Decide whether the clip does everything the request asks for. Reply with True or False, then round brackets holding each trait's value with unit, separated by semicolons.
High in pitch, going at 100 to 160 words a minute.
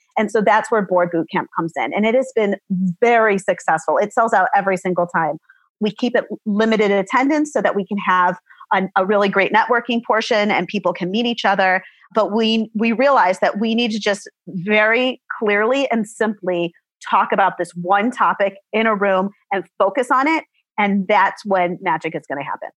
False (205 Hz; 200 wpm)